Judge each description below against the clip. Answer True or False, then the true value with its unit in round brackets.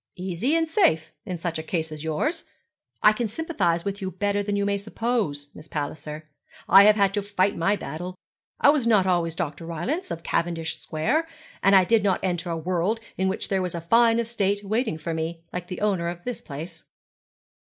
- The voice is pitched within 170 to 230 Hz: True (185 Hz)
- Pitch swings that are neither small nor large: True (4.2 semitones)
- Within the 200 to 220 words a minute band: True (205 wpm)